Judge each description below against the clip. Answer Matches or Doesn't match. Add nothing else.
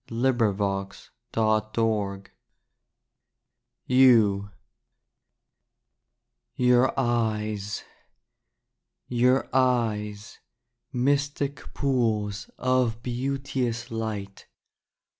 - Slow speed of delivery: Matches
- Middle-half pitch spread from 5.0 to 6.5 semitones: Doesn't match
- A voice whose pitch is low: Matches